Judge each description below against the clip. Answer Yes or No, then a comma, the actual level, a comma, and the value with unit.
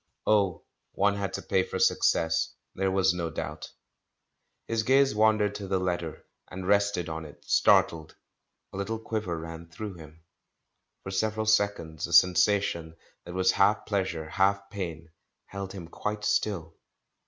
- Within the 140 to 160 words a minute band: Yes, average, 150 wpm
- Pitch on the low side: Yes, very low, 95 Hz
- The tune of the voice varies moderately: Yes, average, 3.7 semitones